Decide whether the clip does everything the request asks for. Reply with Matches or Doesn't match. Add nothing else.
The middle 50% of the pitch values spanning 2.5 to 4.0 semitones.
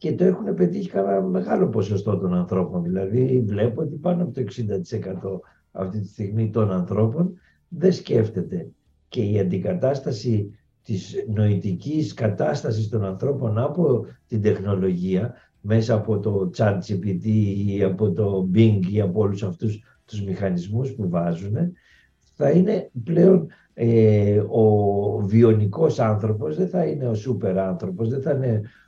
Doesn't match